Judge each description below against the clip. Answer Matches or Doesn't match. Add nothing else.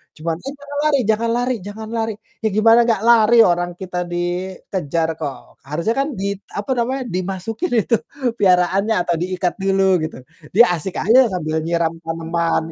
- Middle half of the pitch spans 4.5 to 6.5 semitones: Matches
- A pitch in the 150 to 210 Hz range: Matches